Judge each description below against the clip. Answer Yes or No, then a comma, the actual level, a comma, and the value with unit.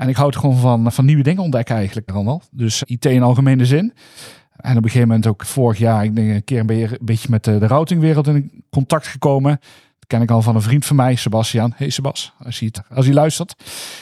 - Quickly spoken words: Yes, fast, 235 wpm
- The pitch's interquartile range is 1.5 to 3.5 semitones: No, average, 4.0 semitones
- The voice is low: Yes, low, 125 Hz